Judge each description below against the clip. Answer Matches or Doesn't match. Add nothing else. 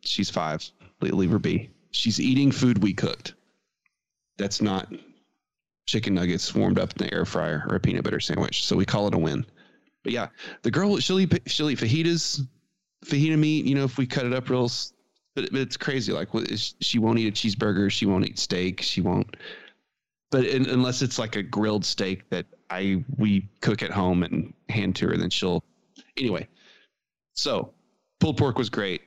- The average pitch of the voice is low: Matches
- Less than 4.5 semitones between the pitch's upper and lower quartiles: Doesn't match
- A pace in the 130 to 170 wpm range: Doesn't match